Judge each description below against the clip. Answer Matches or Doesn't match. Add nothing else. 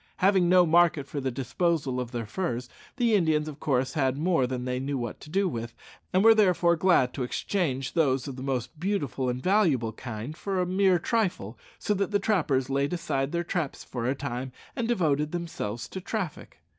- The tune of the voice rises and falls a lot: Matches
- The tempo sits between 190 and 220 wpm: Matches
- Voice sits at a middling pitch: Matches